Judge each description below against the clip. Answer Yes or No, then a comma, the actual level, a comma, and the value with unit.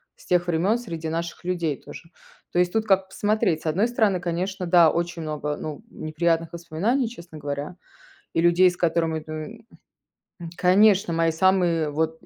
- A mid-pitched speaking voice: Yes, medium, 170 Hz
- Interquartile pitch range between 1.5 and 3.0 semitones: Yes, average, 2.7 semitones